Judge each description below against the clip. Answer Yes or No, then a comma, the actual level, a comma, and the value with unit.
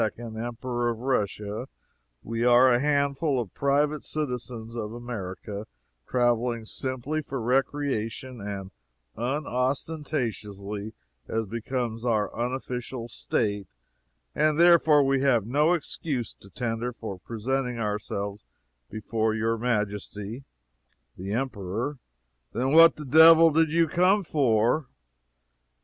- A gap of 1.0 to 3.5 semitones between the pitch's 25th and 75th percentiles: No, average, 4.0 semitones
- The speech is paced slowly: Yes, slow, 110 wpm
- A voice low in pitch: Yes, low, 120 Hz